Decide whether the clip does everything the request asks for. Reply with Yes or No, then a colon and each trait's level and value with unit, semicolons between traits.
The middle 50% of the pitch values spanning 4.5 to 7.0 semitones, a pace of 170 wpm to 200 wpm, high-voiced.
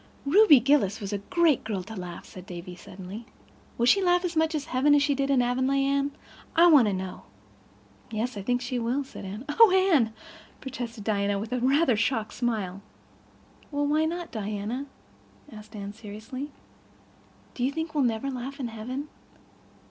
Yes: average, 5.2 semitones; average, 180 wpm; very high, 250 Hz